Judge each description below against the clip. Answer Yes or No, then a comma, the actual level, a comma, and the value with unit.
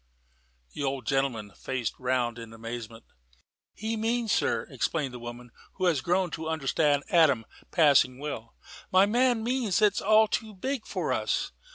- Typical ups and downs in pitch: No, wide, 9.0 semitones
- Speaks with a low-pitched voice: No, medium, 145 Hz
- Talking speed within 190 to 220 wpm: No, average, 160 wpm